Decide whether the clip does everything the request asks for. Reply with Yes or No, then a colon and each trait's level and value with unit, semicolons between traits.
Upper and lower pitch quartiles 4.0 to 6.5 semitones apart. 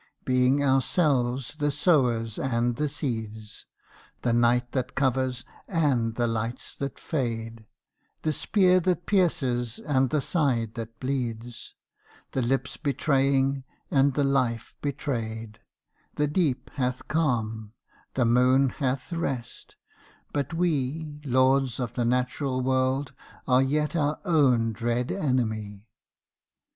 No: average, 3.3 semitones